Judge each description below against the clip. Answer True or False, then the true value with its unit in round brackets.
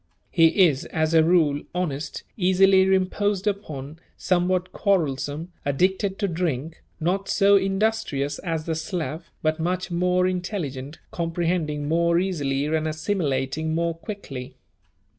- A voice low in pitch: False (170 Hz)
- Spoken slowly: True (125 wpm)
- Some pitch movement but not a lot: True (3.3 semitones)